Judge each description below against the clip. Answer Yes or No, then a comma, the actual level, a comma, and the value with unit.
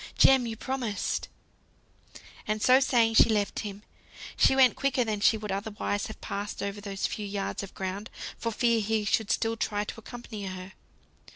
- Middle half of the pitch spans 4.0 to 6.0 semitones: No, narrow, 2.4 semitones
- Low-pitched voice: No, high, 215 Hz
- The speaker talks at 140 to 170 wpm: No, average, 180 wpm